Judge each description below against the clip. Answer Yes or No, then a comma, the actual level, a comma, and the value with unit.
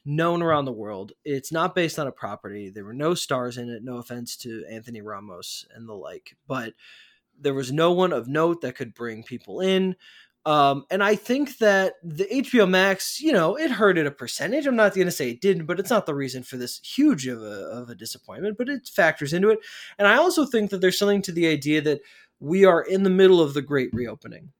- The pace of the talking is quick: Yes, fast, 235 wpm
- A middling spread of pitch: No, wide, 7.4 semitones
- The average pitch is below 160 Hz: No, medium, 165 Hz